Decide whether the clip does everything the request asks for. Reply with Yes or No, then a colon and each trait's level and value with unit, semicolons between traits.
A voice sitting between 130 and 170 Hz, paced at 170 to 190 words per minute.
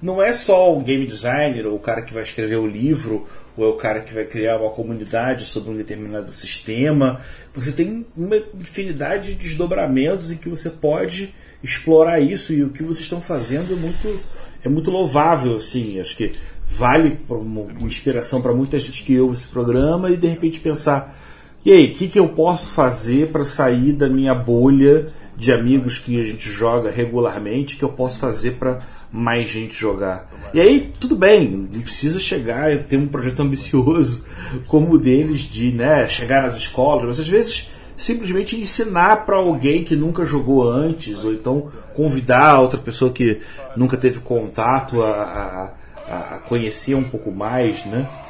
Yes: low, 135 Hz; average, 180 wpm